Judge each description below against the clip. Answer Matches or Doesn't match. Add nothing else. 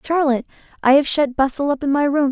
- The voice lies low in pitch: Doesn't match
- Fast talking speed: Matches